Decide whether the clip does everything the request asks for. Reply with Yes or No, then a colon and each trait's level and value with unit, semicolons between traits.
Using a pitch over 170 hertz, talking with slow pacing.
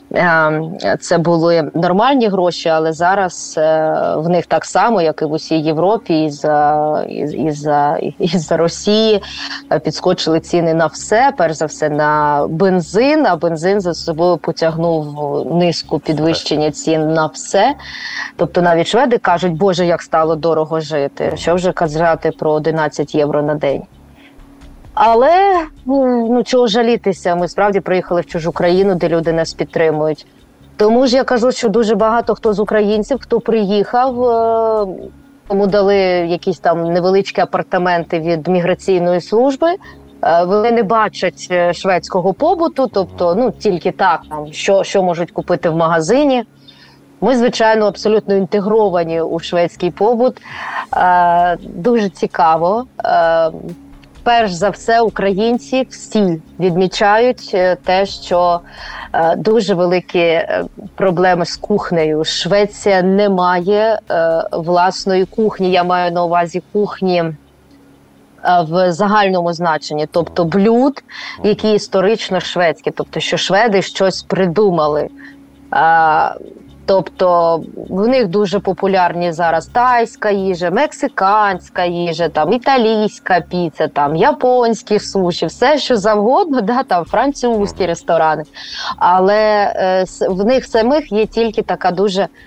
No: medium, 185 Hz; average, 120 wpm